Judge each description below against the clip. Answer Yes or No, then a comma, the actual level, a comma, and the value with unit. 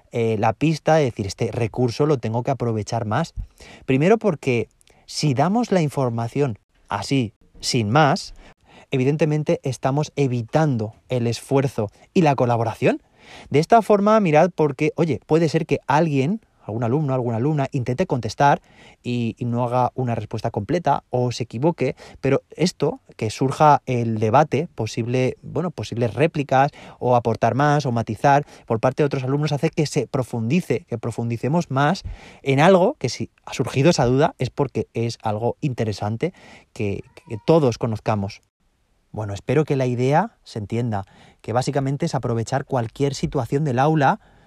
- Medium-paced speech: Yes, average, 155 wpm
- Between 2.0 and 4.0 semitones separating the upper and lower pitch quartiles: No, average, 4.4 semitones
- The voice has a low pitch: Yes, low, 130 Hz